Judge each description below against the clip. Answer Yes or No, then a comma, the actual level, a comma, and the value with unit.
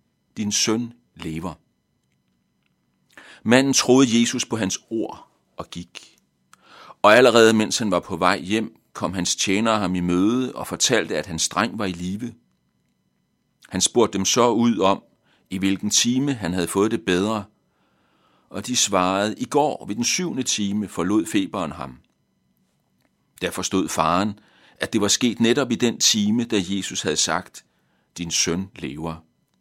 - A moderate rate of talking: Yes, average, 155 wpm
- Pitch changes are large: No, average, 4.9 semitones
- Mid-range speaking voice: No, low, 100 Hz